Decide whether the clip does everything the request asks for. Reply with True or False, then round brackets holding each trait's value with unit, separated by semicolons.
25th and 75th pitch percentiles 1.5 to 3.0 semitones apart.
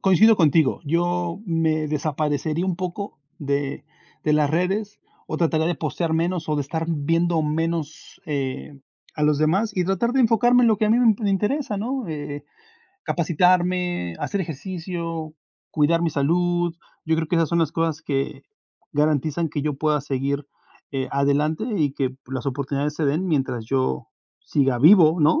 False (3.5 semitones)